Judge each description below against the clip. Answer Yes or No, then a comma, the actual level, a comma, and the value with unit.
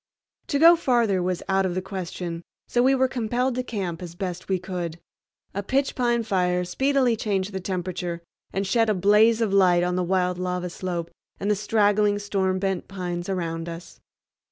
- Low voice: No, high, 190 Hz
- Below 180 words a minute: No, average, 185 wpm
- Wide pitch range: No, average, 3.5 semitones